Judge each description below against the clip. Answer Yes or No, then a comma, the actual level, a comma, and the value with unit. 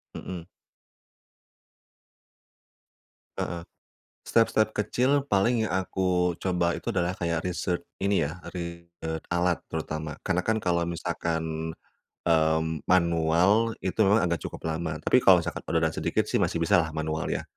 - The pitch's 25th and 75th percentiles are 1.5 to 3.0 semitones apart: Yes, narrow, 2.6 semitones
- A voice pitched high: No, very low, 85 Hz